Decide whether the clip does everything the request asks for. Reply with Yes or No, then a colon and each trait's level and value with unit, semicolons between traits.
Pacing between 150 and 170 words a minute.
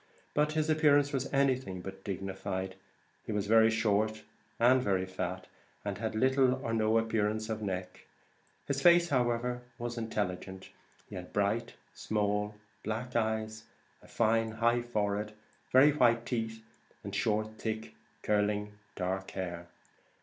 No: slow, 135 wpm